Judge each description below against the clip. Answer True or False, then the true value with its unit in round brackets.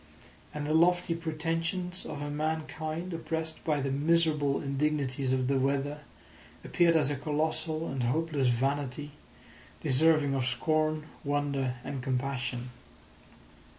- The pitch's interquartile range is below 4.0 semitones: True (2.8 semitones)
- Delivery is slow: True (120 wpm)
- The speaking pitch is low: False (150 Hz)